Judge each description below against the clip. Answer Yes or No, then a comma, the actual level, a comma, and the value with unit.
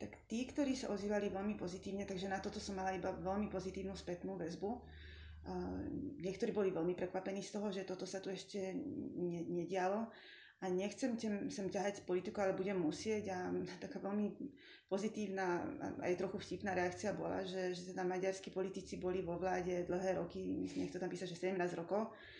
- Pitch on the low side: No, high, 190 Hz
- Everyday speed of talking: No, fast, 180 wpm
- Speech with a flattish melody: Yes, narrow, 2.0 semitones